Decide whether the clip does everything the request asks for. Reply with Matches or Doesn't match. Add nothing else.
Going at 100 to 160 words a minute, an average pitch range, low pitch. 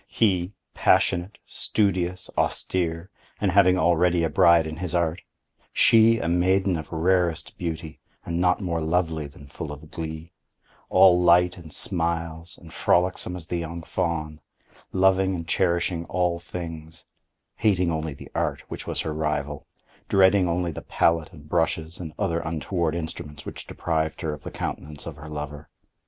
Doesn't match